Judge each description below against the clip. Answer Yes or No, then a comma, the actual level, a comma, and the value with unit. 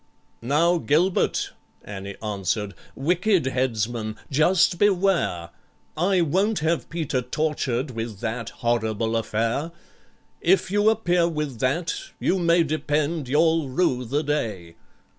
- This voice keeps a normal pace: No, slow, 115 wpm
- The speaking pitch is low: No, medium, 145 Hz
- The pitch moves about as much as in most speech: No, wide, 6.7 semitones